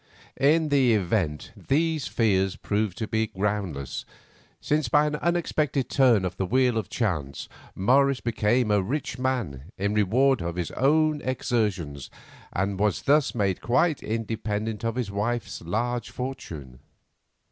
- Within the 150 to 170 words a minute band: No, average, 140 wpm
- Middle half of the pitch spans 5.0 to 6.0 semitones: Yes, average, 5.3 semitones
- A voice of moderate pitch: No, low, 110 Hz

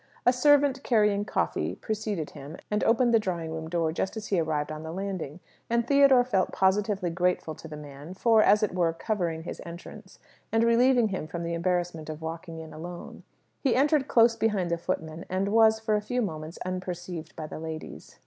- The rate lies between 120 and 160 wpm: No, average, 195 wpm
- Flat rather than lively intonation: No, average, 5.3 semitones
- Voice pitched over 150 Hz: Yes, medium, 185 Hz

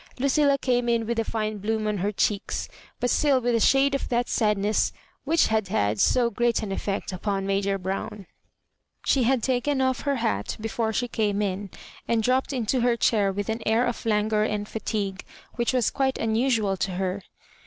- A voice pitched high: Yes, high, 220 Hz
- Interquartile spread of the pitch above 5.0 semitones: No, average, 3.2 semitones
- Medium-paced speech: Yes, average, 190 wpm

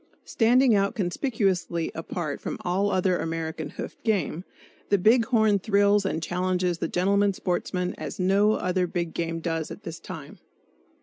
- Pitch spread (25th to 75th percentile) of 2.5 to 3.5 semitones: Yes, average, 3.0 semitones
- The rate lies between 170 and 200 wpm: No, average, 150 wpm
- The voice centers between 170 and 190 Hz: Yes, medium, 185 Hz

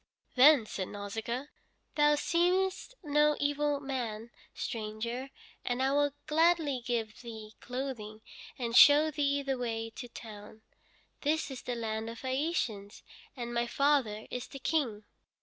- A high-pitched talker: Yes, very high, 255 Hz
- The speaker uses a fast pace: No, average, 140 wpm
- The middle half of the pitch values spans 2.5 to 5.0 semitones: Yes, average, 4.4 semitones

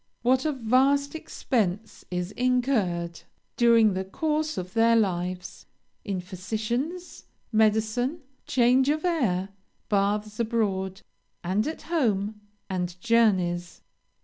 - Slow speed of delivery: Yes, slow, 105 wpm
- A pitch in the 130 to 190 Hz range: No, high, 220 Hz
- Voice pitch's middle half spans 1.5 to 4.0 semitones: No, average, 5.2 semitones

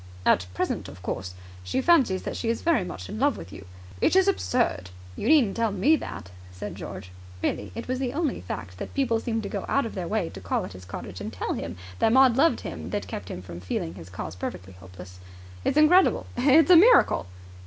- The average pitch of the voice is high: Yes, high, 195 Hz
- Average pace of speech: No, fast, 225 wpm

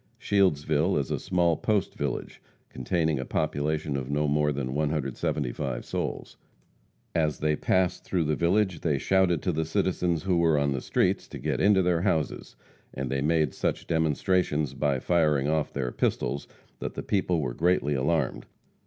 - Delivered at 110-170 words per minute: Yes, average, 165 wpm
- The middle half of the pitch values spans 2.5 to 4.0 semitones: Yes, average, 3.6 semitones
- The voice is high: No, very low, 75 Hz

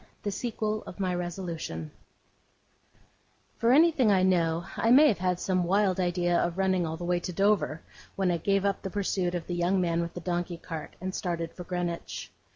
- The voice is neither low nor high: Yes, medium, 180 Hz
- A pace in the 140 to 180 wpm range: No, average, 195 wpm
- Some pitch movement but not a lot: No, narrow, 2.2 semitones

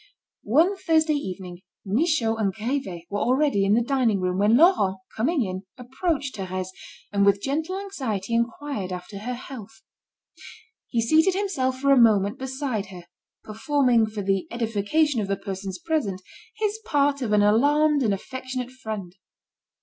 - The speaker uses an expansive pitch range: Yes, wide, 6.1 semitones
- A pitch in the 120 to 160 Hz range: No, high, 235 Hz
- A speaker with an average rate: Yes, average, 150 wpm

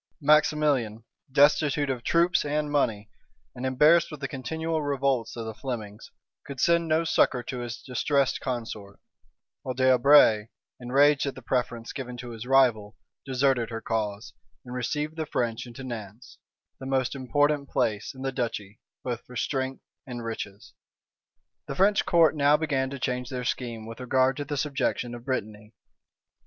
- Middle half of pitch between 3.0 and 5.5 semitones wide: Yes, average, 3.5 semitones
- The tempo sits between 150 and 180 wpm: Yes, average, 160 wpm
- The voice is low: Yes, low, 130 Hz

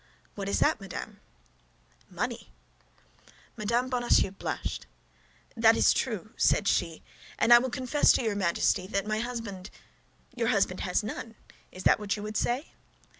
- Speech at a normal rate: Yes, average, 155 wpm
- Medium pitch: No, high, 215 Hz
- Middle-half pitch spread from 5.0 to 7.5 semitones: No, average, 3.4 semitones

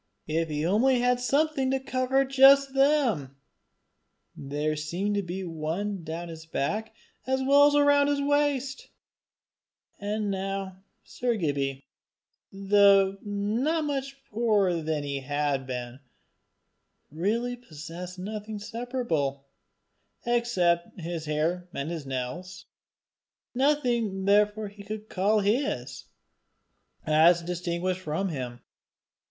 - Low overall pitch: No, high, 195 Hz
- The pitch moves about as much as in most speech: No, wide, 7.3 semitones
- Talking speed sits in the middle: No, slow, 115 wpm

